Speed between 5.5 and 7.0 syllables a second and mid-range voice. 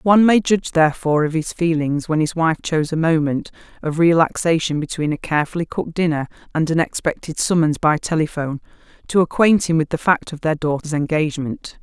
Yes: 6.0 syllables/s; medium, 160 Hz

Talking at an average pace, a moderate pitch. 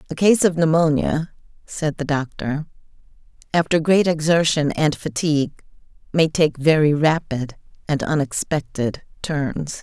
No: slow, 115 wpm; medium, 155 Hz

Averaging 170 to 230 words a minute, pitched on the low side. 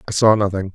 No: fast, 245 wpm; low, 100 Hz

